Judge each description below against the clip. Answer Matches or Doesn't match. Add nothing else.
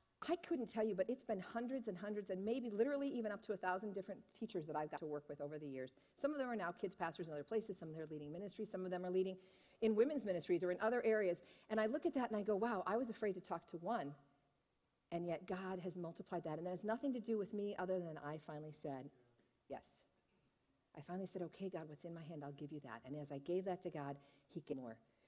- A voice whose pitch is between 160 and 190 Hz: Matches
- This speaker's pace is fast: Matches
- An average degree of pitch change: Doesn't match